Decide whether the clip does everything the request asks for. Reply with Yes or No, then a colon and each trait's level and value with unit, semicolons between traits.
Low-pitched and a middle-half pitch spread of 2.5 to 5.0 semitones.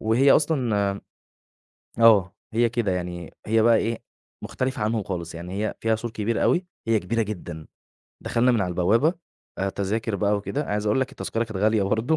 Yes: low, 110 Hz; average, 2.9 semitones